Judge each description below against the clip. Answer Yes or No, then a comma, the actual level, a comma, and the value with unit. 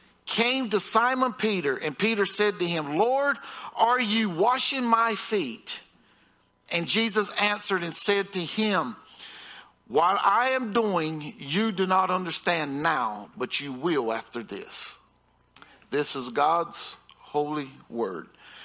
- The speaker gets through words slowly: Yes, slow, 130 wpm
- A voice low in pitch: No, high, 200 Hz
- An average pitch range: No, wide, 6.3 semitones